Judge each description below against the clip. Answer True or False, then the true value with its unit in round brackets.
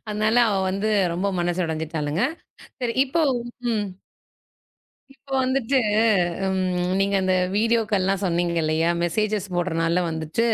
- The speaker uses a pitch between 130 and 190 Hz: True (185 Hz)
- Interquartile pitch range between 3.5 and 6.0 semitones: True (4.0 semitones)